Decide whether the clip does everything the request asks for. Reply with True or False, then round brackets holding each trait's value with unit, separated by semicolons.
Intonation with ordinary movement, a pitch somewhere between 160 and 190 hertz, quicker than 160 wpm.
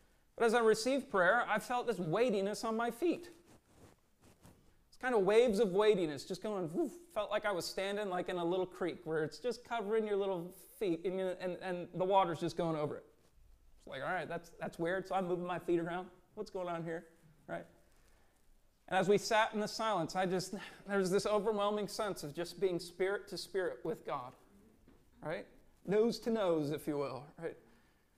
True (4.2 semitones; 185 Hz; 200 wpm)